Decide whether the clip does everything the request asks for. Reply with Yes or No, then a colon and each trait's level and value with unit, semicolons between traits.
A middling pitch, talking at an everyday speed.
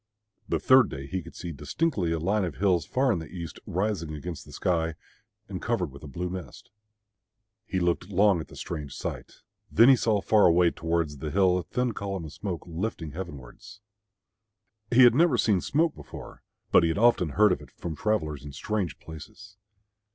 No: very low, 90 Hz; average, 195 wpm